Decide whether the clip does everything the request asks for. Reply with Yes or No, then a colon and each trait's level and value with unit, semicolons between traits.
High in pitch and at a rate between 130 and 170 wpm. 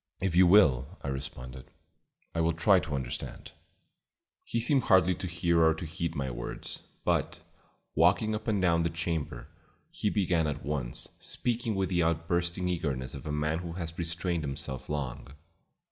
No: very low, 85 Hz; average, 165 wpm